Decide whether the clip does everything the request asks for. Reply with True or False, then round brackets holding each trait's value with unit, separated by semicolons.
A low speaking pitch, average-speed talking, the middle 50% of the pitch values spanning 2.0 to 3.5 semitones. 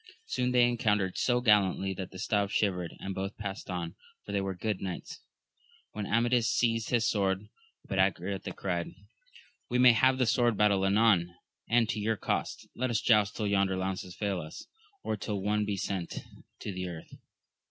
True (105 Hz; 180 wpm; 3.1 semitones)